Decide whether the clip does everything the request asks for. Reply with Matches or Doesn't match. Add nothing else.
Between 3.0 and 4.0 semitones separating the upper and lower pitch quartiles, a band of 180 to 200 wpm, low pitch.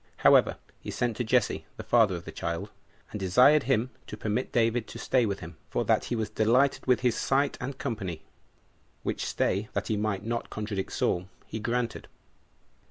Matches